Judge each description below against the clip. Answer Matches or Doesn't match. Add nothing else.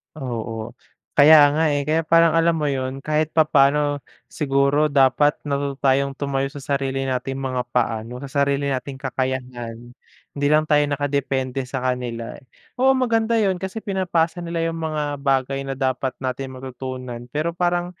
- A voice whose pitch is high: Doesn't match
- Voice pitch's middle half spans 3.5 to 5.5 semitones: Doesn't match